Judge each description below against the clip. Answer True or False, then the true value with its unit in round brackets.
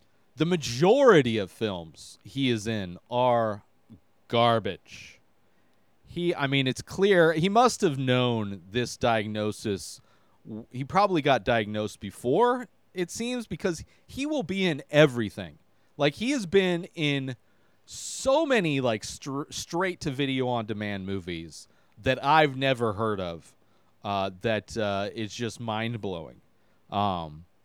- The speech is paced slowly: True (130 wpm)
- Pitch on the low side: True (120 Hz)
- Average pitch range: False (6.9 semitones)